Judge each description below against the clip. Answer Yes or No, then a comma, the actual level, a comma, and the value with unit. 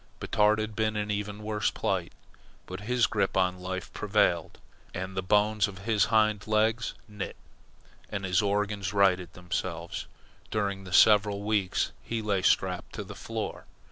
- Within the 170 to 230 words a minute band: No, average, 155 wpm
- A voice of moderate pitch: No, low, 105 Hz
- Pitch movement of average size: No, narrow, 2.2 semitones